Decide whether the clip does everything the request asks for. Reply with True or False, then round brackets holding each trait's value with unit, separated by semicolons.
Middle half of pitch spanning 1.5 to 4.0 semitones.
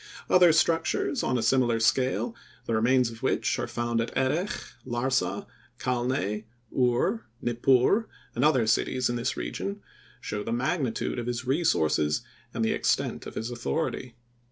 True (2.5 semitones)